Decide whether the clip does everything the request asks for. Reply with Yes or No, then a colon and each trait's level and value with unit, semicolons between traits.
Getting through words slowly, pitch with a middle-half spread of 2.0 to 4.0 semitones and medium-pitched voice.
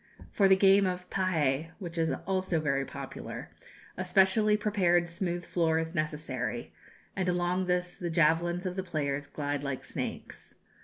No: average, 155 wpm; average, 3.2 semitones; medium, 175 Hz